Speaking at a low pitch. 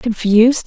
No: high, 225 Hz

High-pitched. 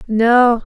Yes: high, 235 Hz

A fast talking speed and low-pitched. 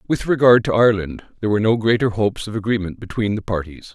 Yes: fast, 215 wpm; low, 105 Hz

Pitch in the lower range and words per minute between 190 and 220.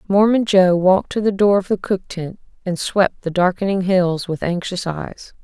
No: medium, 185 Hz; average, 200 wpm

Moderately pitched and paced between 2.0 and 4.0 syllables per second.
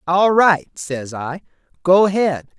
Yes: medium, 165 Hz; 3.6 syllables/s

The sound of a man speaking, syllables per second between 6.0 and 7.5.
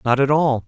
No: male; 5.5 syllables/s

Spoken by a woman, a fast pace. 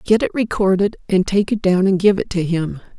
Yes: female; fast, 240 wpm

